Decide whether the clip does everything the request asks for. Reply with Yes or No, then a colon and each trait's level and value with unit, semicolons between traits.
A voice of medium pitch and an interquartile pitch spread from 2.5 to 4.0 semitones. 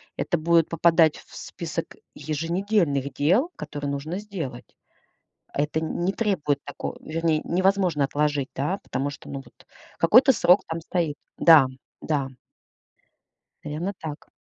Yes: medium, 160 Hz; average, 3.7 semitones